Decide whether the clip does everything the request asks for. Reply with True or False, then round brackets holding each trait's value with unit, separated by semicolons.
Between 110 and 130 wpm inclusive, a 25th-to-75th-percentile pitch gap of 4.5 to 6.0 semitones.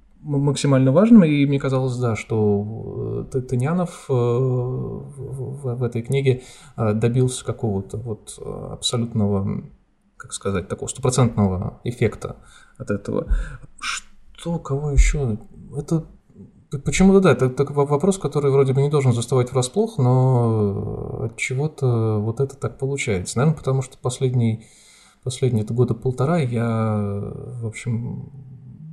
False (115 wpm; 3.4 semitones)